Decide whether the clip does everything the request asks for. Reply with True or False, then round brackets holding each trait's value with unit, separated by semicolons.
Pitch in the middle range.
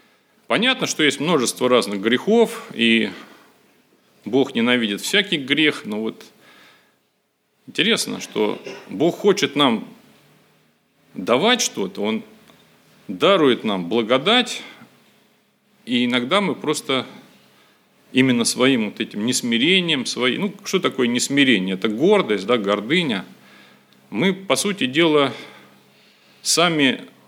True (145 Hz)